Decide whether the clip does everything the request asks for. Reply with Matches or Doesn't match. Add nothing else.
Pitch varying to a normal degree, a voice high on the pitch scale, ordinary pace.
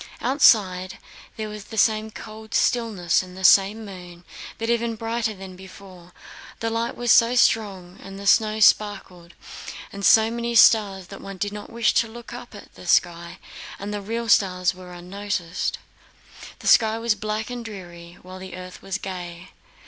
Matches